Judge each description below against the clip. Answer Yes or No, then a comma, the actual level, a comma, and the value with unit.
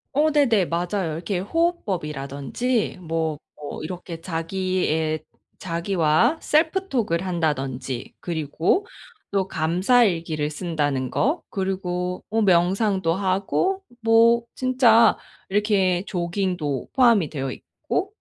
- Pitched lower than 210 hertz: Yes, medium, 185 Hz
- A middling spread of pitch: No, wide, 5.7 semitones